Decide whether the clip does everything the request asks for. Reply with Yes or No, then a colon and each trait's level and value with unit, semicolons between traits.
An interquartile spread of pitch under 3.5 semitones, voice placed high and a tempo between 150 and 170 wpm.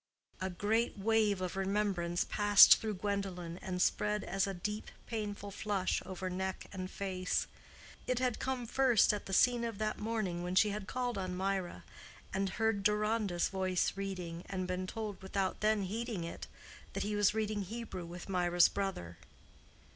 Yes: narrow, 2.6 semitones; high, 195 Hz; average, 165 wpm